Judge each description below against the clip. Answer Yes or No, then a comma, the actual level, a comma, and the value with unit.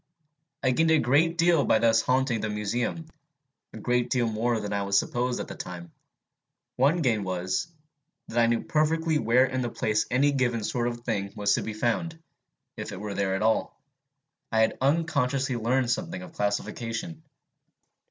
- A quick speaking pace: No, average, 175 wpm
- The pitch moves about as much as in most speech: Yes, average, 4.7 semitones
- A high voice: No, low, 120 Hz